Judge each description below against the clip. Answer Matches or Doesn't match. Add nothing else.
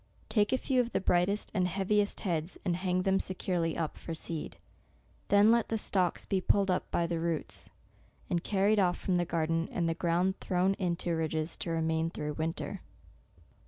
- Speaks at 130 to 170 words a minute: Doesn't match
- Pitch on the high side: Doesn't match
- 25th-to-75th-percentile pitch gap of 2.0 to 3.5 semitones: Matches